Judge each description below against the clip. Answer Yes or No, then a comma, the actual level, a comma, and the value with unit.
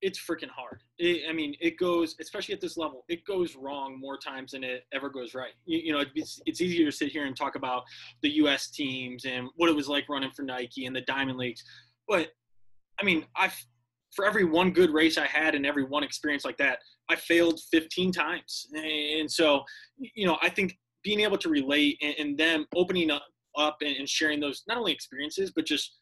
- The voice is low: No, medium, 150 Hz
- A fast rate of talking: Yes, fast, 215 wpm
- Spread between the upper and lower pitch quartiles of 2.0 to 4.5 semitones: Yes, average, 3.9 semitones